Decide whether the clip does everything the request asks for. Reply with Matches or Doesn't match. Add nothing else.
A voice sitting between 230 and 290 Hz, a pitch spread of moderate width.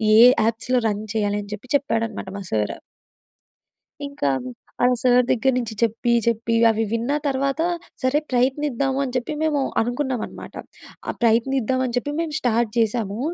Matches